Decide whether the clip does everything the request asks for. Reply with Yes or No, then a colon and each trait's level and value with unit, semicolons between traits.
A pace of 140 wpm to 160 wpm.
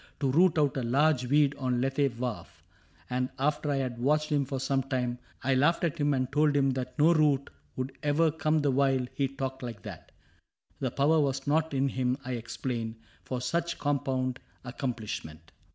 No: average, 185 wpm